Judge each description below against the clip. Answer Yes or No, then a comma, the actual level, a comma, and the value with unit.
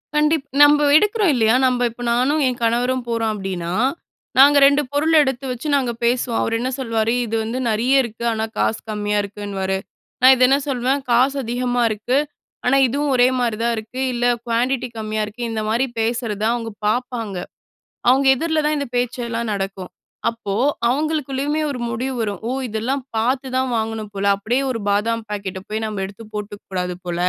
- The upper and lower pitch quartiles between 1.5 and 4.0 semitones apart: Yes, average, 3.4 semitones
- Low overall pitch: No, high, 235 Hz